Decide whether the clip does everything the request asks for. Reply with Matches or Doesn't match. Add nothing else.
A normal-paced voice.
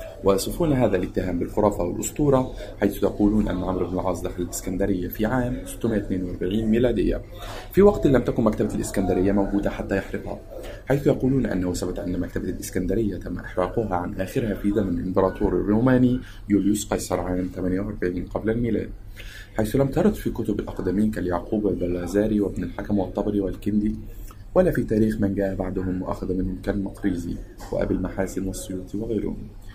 Doesn't match